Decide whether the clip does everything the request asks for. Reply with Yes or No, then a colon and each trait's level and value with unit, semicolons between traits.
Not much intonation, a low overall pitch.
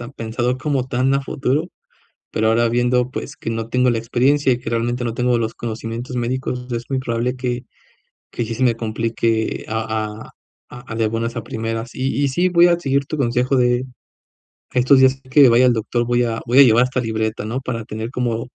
Yes: narrow, 2.2 semitones; low, 120 Hz